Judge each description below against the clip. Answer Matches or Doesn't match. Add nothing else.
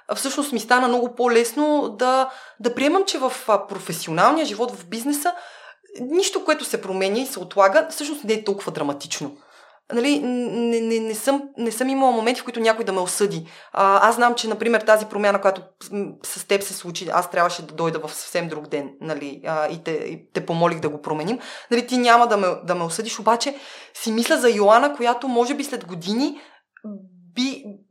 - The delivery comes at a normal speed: Doesn't match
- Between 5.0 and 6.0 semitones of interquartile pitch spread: Matches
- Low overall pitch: Doesn't match